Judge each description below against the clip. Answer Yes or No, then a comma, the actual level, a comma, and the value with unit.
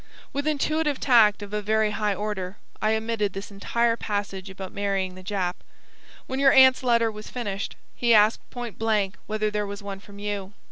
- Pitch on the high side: Yes, high, 210 Hz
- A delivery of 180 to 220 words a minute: Yes, average, 185 wpm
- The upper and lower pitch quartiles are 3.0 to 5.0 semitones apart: No, narrow, 2.6 semitones